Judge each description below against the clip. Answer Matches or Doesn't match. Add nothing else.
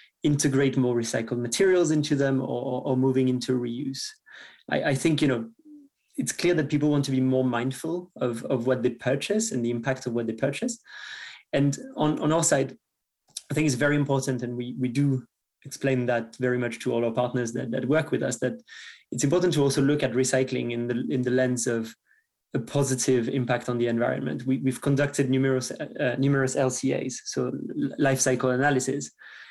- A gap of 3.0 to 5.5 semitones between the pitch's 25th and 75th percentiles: Doesn't match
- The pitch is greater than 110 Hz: Matches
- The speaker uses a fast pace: Doesn't match